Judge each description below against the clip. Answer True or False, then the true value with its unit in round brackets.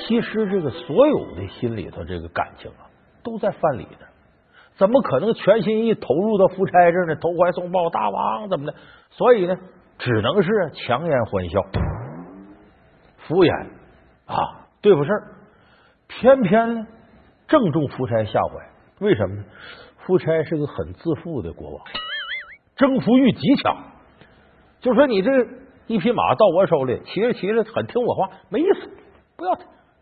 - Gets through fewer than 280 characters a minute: True (225 characters per minute)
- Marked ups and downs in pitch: True (6.7 semitones)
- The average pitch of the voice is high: True (195 Hz)